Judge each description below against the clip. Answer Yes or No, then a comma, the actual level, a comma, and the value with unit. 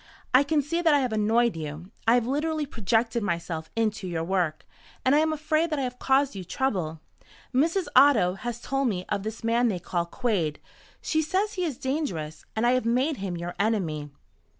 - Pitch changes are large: Yes, wide, 7.6 semitones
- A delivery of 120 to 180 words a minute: No, average, 200 wpm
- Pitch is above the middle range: Yes, high, 235 Hz